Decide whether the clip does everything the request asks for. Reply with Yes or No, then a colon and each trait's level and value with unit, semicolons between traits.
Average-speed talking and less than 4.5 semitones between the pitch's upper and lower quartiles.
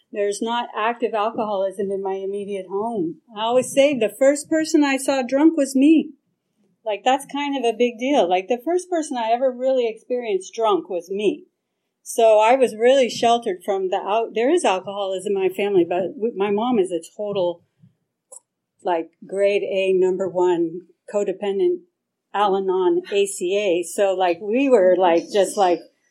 No: average, 170 wpm; average, 5.0 semitones